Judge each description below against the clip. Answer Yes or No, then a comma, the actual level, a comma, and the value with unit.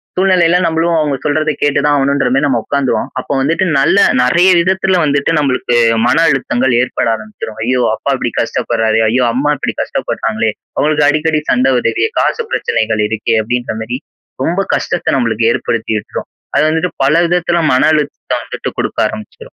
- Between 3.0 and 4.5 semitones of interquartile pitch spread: No, average, 5.1 semitones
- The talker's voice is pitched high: No, medium, 140 Hz